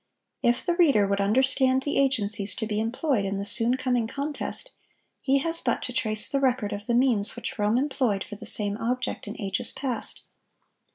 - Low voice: No, high, 240 Hz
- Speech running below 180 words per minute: No, average, 190 wpm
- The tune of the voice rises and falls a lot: No, average, 4.2 semitones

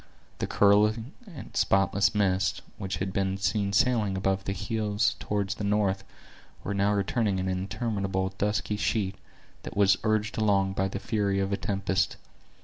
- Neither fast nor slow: Yes, average, 160 wpm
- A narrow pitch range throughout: Yes, narrow, 1.4 semitones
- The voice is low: Yes, low, 100 Hz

